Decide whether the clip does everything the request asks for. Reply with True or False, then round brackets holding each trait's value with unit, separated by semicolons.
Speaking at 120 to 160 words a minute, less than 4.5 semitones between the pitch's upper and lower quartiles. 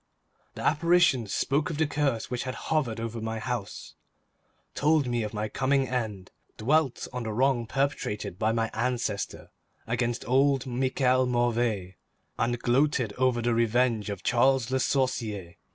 True (150 wpm; 3.0 semitones)